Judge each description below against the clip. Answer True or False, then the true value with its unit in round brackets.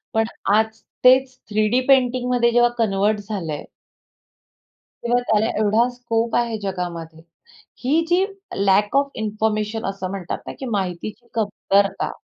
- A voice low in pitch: False (220 Hz)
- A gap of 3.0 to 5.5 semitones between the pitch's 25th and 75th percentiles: True (3.5 semitones)